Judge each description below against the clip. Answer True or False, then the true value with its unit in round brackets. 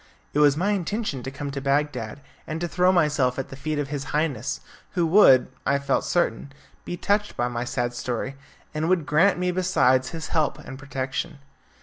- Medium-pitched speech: True (145 Hz)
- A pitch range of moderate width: True (4.4 semitones)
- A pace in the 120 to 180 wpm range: False (195 wpm)